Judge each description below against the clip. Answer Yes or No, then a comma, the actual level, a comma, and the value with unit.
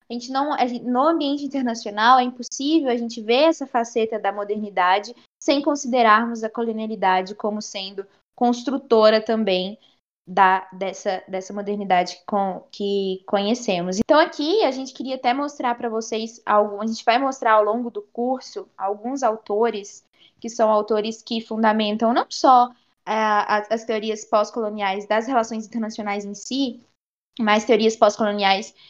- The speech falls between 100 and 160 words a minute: Yes, average, 145 wpm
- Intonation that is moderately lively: Yes, average, 3.0 semitones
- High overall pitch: Yes, high, 225 Hz